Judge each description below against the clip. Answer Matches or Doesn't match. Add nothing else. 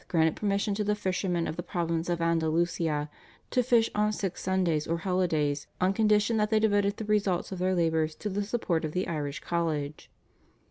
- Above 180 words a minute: Matches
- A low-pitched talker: Doesn't match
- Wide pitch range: Doesn't match